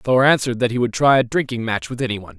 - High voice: No, low, 125 Hz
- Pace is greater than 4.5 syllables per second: Yes, 7.2 syllables/s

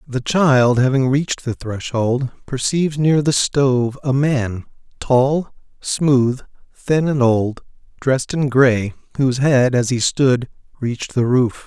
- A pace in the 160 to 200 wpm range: No, average, 145 wpm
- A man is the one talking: Yes, male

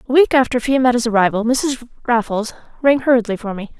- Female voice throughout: Yes, female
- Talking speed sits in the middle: Yes, average, 175 wpm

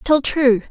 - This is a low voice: No, very high, 260 Hz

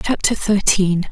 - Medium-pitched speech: No, high, 195 Hz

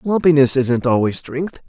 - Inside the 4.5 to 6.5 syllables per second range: Yes, 4.6 syllables/s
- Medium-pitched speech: Yes, medium, 145 Hz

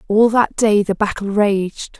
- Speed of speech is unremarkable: Yes, average, 180 wpm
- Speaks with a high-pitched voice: Yes, high, 205 Hz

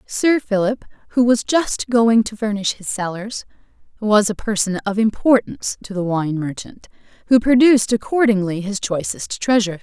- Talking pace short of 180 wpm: Yes, average, 155 wpm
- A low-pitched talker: No, high, 215 Hz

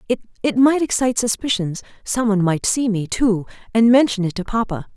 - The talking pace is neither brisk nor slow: Yes, average, 180 wpm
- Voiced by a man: No, female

